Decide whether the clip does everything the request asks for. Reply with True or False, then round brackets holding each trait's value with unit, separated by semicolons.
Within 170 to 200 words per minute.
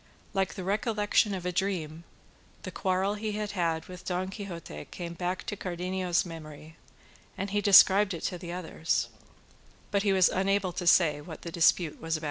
True (180 wpm)